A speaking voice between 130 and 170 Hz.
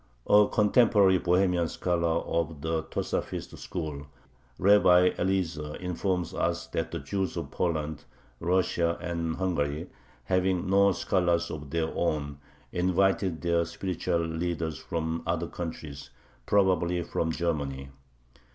No: very low, 85 Hz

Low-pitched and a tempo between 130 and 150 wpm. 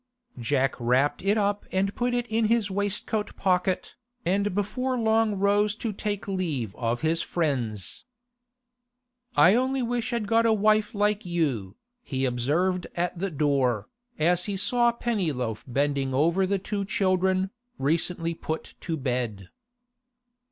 No: medium, 185 Hz; average, 140 wpm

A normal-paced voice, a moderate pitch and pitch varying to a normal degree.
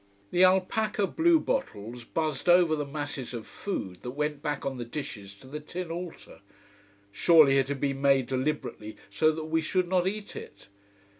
Yes: average, 175 wpm; medium, 150 Hz; average, 5.0 semitones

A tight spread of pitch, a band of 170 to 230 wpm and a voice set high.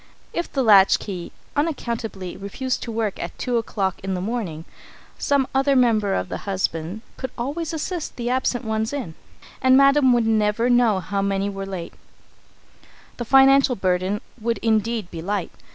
No: average, 4.9 semitones; average, 180 wpm; high, 225 Hz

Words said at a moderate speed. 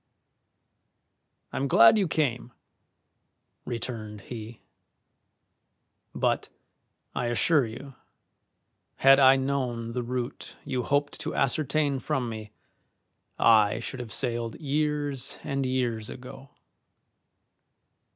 No: slow, 95 wpm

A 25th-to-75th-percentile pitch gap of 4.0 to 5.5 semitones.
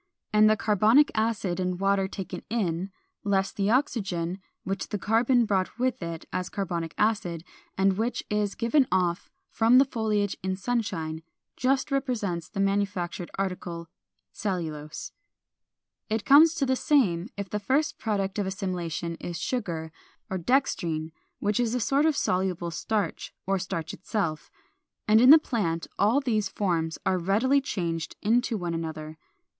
Yes: average, 4.7 semitones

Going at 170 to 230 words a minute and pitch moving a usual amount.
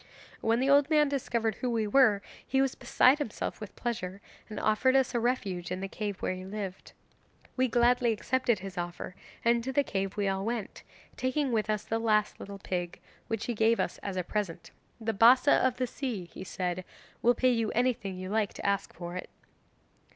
Yes: average, 200 wpm; average, 4.2 semitones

